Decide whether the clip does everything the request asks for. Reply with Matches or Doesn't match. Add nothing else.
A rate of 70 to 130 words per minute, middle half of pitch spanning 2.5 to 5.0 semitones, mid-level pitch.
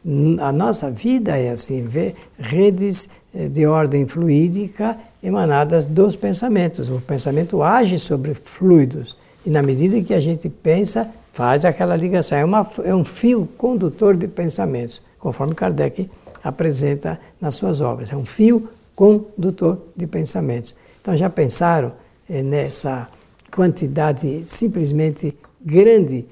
Doesn't match